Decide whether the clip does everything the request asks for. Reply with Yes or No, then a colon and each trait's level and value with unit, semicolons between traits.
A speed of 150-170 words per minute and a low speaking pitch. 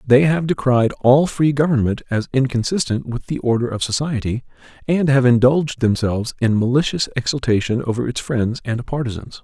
Yes: average, 160 wpm; low, 125 Hz